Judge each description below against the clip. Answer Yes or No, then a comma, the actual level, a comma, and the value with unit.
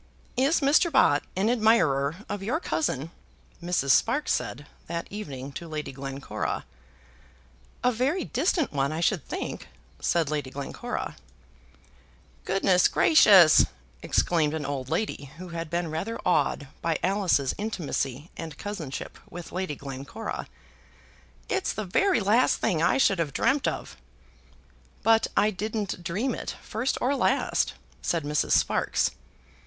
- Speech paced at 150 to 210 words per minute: No, slow, 135 wpm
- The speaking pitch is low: No, medium, 175 Hz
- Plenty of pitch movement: Yes, wide, 7.0 semitones